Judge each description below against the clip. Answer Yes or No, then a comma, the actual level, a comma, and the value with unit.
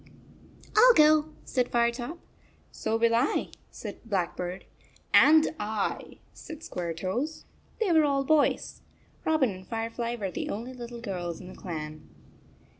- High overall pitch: Yes, high, 235 Hz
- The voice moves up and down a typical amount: No, wide, 7.9 semitones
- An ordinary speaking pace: No, slow, 130 wpm